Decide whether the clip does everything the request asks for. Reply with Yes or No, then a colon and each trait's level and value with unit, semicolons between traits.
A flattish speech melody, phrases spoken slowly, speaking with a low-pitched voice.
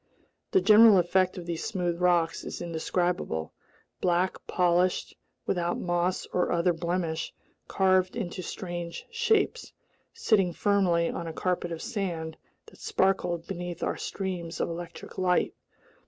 No: narrow, 1.7 semitones; slow, 130 wpm; medium, 180 Hz